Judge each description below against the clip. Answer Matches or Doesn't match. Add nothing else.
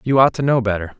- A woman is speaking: Doesn't match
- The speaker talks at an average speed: Doesn't match